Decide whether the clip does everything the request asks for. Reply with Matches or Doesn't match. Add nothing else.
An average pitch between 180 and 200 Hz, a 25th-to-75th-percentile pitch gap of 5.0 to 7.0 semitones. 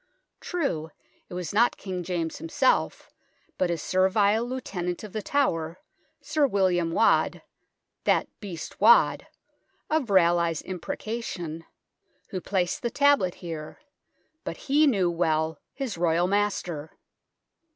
Matches